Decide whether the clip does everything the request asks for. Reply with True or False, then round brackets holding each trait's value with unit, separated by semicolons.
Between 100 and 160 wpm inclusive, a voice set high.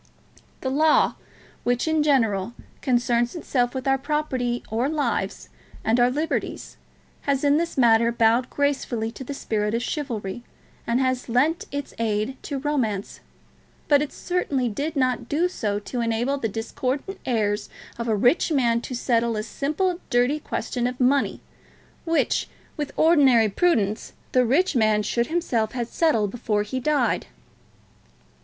True (150 wpm; 250 Hz)